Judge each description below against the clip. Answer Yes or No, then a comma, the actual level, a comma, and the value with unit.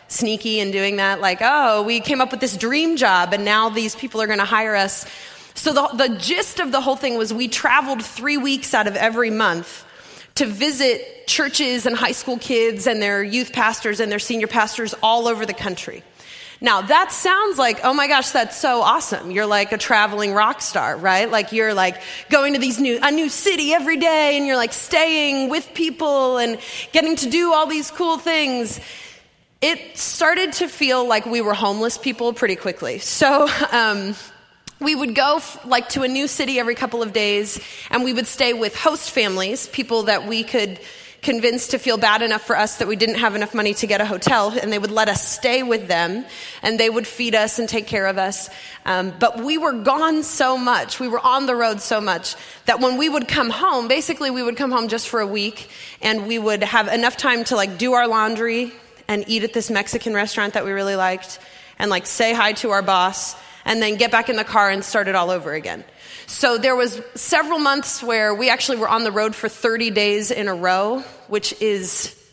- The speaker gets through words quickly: Yes, fast, 220 wpm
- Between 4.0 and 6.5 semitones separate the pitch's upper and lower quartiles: Yes, average, 4.3 semitones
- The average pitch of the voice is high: Yes, high, 235 Hz